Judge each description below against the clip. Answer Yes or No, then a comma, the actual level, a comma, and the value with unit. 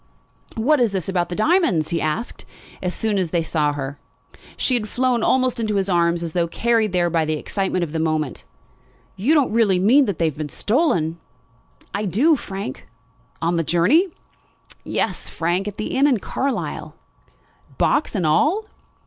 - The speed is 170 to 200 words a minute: Yes, average, 175 wpm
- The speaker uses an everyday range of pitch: No, wide, 6.1 semitones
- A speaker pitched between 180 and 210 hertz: Yes, high, 190 Hz